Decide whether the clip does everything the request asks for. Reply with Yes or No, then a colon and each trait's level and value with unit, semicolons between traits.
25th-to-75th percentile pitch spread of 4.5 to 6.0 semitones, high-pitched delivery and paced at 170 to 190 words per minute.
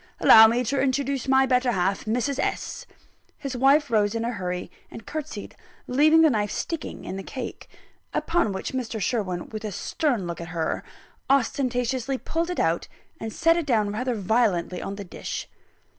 Yes: average, 5.0 semitones; high, 240 Hz; average, 175 wpm